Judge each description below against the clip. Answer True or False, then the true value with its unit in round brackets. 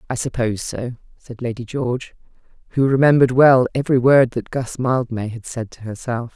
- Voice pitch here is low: True (125 Hz)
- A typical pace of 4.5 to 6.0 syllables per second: True (5.5 syllables/s)